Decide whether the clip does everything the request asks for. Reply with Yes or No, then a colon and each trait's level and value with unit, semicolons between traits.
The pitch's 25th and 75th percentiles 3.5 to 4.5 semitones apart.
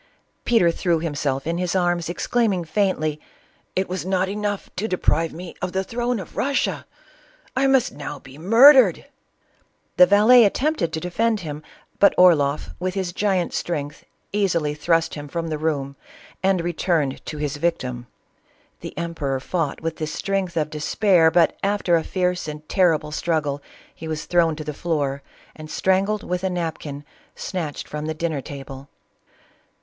Yes: average, 3.8 semitones